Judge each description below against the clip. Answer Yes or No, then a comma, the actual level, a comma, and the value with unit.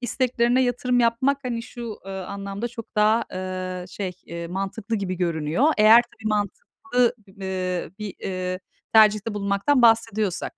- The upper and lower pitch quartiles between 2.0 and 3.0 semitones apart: No, average, 4.0 semitones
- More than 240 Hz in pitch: No, high, 210 Hz